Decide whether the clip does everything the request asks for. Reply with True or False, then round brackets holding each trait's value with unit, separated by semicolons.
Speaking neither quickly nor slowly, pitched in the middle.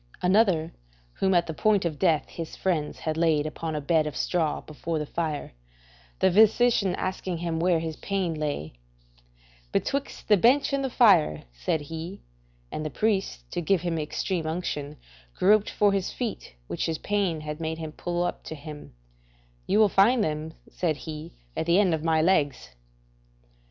True (175 wpm; 165 Hz)